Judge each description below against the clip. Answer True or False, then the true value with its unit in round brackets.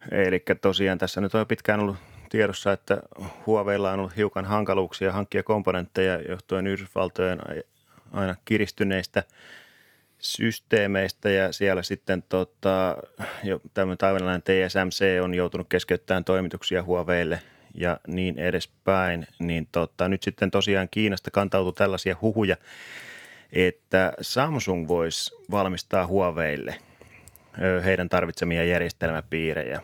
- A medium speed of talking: True (110 wpm)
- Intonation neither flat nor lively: False (1.5 semitones)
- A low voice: True (95 Hz)